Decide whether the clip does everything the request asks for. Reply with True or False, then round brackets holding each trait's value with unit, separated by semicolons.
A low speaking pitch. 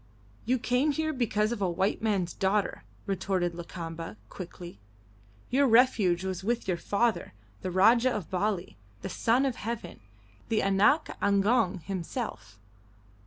False (200 Hz)